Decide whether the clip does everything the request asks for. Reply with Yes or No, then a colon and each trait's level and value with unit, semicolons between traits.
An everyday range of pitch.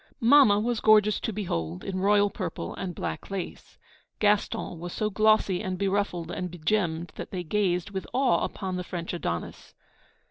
Yes: average, 3.0 semitones